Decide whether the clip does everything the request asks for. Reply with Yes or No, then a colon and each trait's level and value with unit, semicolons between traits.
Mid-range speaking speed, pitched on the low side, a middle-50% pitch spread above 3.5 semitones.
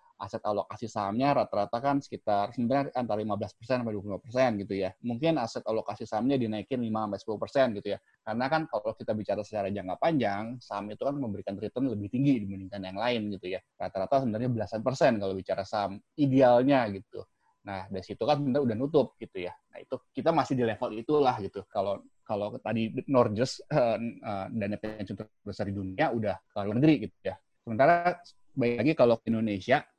Yes: average, 180 wpm; low, 110 Hz; average, 4.1 semitones